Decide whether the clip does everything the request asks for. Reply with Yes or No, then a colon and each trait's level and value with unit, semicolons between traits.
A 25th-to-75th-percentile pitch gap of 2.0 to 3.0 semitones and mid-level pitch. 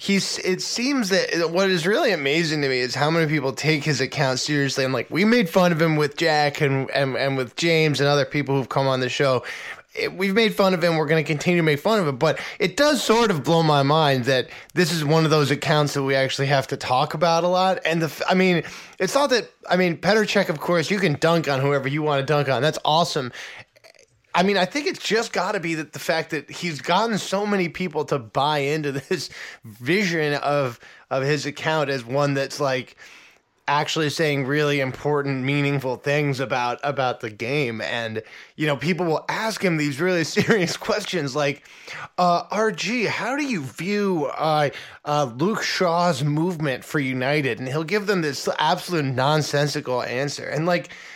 No: average, 4.3 semitones; medium, 155 Hz